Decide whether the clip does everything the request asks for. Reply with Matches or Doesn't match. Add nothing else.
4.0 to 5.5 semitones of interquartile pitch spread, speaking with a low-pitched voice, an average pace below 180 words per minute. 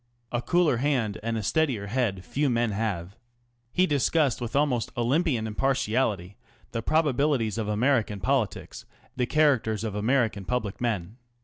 Matches